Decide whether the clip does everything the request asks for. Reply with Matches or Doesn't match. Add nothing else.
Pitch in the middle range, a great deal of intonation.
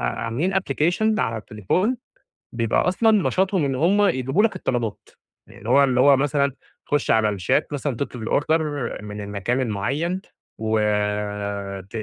Doesn't match